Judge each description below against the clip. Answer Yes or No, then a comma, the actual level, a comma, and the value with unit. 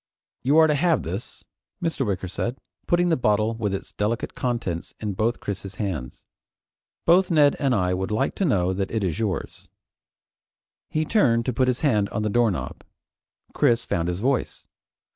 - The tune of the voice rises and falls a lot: Yes, wide, 5.8 semitones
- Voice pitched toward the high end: No, low, 115 Hz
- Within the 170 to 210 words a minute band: Yes, average, 175 wpm